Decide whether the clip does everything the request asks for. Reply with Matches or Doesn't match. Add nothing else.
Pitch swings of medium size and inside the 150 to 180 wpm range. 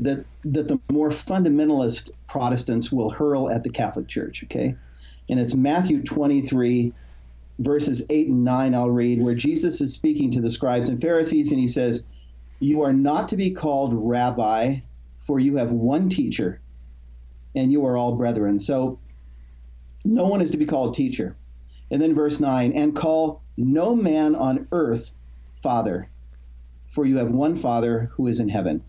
Doesn't match